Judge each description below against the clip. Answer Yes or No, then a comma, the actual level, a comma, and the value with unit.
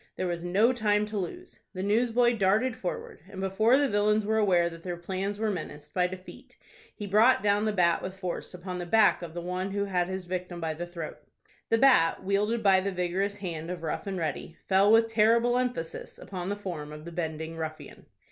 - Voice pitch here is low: No, high, 190 Hz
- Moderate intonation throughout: Yes, average, 3.4 semitones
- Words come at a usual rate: No, fast, 215 wpm